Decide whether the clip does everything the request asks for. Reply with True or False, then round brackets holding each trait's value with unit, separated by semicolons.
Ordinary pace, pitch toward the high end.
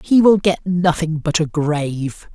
False (180 wpm; 165 Hz)